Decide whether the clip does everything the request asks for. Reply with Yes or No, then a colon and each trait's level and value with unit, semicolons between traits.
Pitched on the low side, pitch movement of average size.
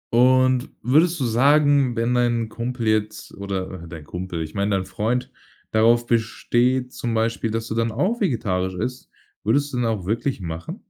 Yes: low, 115 Hz; average, 3.5 semitones